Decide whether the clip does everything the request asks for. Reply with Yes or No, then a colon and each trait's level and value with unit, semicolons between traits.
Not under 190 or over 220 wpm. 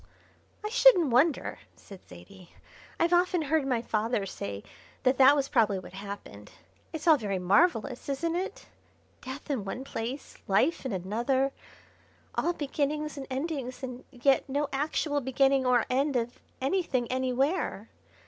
No: average, 145 wpm